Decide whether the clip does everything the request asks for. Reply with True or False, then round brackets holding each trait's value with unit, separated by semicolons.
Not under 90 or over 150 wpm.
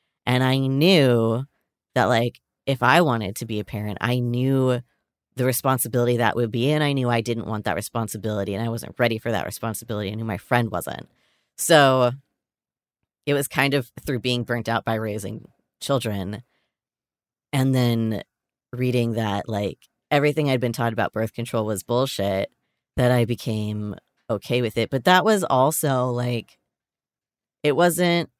False (165 wpm)